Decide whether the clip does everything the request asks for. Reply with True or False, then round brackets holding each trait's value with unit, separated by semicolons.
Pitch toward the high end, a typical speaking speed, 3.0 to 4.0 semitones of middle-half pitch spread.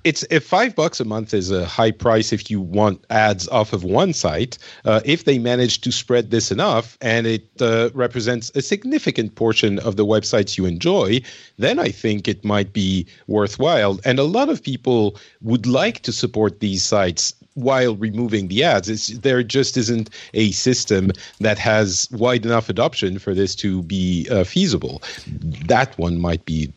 False (110 Hz; 180 wpm; 3.4 semitones)